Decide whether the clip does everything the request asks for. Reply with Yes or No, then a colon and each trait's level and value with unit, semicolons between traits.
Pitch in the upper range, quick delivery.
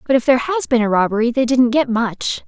Yes: high, 245 Hz; fast, 265 wpm